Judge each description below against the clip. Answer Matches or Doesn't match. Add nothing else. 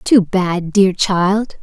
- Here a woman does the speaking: Matches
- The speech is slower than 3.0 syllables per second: Matches